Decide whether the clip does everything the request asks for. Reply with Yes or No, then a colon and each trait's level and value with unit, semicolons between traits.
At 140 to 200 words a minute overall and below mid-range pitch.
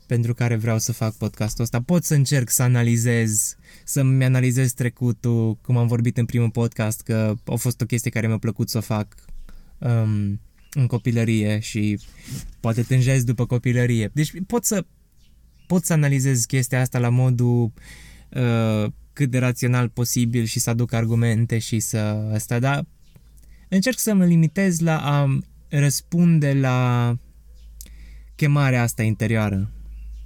Yes: average, 145 wpm; low, 120 Hz